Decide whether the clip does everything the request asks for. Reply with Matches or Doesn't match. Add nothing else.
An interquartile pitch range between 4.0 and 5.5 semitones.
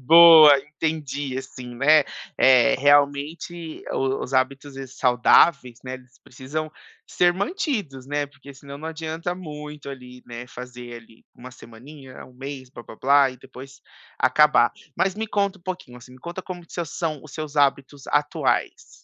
Doesn't match